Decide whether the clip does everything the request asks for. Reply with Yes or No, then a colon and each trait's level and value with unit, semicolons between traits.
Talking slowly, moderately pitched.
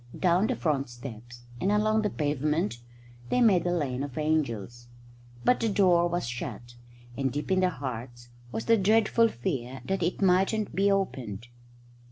No: average, 165 wpm; medium, 155 Hz